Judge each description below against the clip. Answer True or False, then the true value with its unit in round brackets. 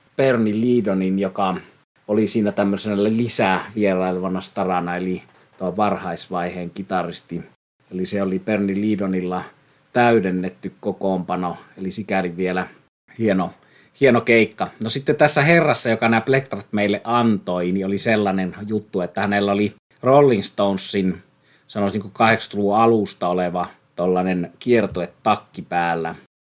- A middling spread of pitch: True (3.3 semitones)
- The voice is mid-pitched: False (100 Hz)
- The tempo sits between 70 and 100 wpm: False (120 wpm)